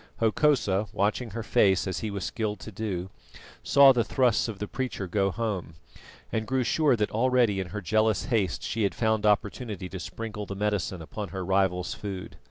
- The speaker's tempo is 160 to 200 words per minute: Yes, average, 185 wpm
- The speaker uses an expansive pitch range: No, average, 2.9 semitones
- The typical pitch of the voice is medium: No, low, 105 Hz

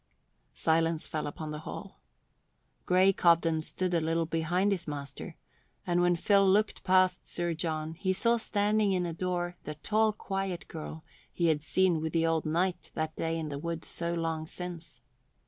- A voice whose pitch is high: No, medium, 170 Hz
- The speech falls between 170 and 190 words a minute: Yes, average, 175 wpm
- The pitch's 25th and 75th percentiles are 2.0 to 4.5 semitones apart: Yes, narrow, 2.6 semitones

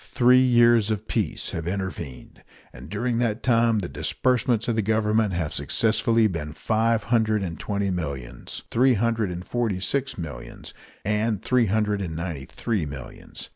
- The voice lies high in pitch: No, low, 105 Hz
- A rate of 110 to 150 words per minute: No, average, 160 wpm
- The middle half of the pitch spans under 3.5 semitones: No, average, 4.7 semitones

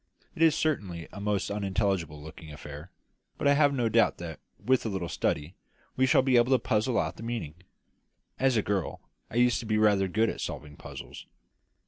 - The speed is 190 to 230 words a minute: Yes, average, 195 wpm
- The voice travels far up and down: Yes, wide, 5.7 semitones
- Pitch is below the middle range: Yes, low, 105 Hz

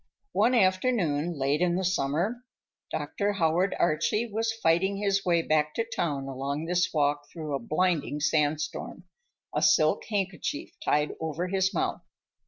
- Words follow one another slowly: No, average, 145 wpm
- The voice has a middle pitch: Yes, medium, 170 Hz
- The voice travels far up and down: No, average, 4.6 semitones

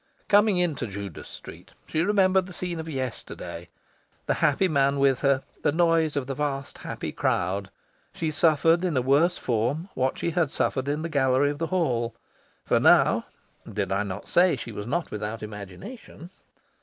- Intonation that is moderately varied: No, wide, 6.0 semitones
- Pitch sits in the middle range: Yes, medium, 145 Hz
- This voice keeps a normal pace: Yes, average, 175 wpm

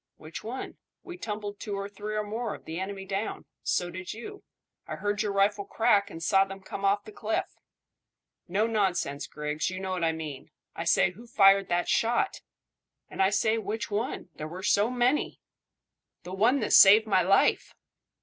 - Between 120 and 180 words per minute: No, average, 190 wpm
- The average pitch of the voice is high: Yes, high, 200 Hz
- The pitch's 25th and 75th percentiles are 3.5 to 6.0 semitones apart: No, average, 2.7 semitones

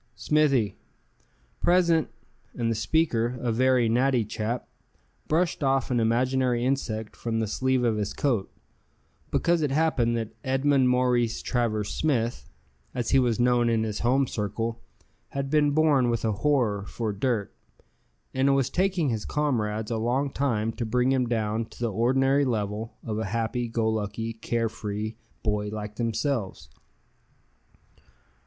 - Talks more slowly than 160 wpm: Yes, average, 150 wpm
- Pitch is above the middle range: No, low, 120 Hz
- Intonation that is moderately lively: Yes, average, 3.3 semitones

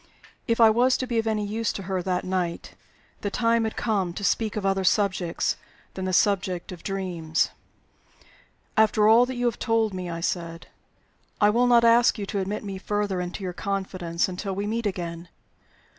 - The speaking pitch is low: No, high, 200 Hz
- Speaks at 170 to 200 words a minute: Yes, average, 195 wpm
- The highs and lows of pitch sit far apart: No, average, 3.4 semitones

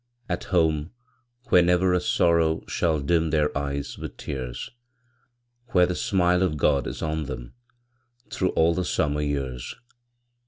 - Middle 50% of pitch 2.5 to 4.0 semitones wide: Yes, average, 3.5 semitones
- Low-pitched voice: Yes, very low, 80 Hz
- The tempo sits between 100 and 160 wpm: Yes, average, 145 wpm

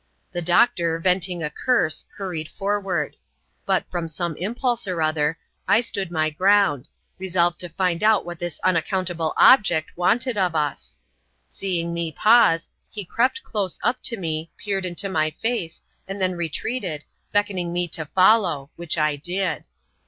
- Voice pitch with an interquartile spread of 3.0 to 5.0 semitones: Yes, average, 3.4 semitones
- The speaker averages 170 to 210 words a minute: No, average, 150 wpm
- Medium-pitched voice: Yes, medium, 175 Hz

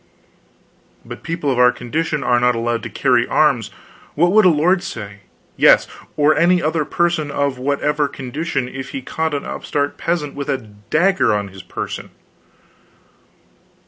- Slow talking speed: No, average, 155 wpm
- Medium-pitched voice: Yes, medium, 145 Hz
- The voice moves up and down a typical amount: Yes, average, 4.7 semitones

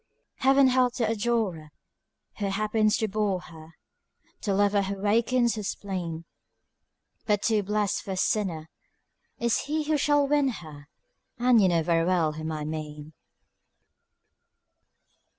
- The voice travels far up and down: Yes, wide, 5.8 semitones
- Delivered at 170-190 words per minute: No, slow, 135 wpm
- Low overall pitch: No, high, 205 Hz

